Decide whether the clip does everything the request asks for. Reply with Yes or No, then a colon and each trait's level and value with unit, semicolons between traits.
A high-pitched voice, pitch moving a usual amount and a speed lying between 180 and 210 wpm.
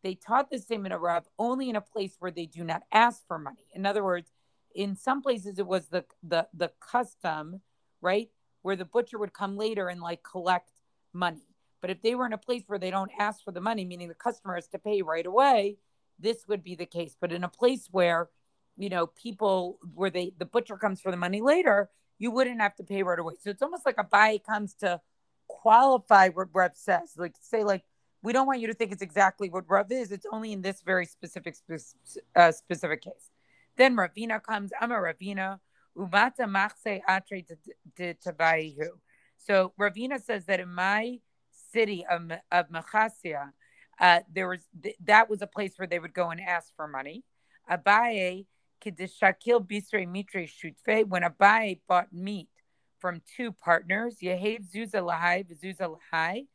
Yes: high, 195 Hz; average, 3.4 semitones; average, 185 wpm